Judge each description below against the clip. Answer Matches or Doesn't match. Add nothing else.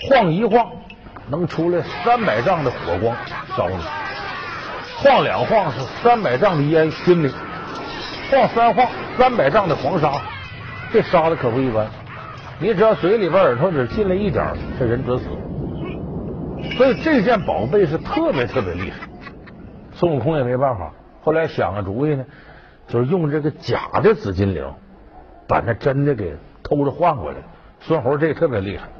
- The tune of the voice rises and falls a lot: Matches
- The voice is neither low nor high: Matches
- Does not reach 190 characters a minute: Doesn't match